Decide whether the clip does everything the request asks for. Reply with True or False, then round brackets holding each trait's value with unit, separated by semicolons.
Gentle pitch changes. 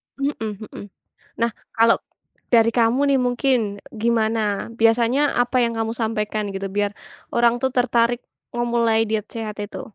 True (1.5 semitones)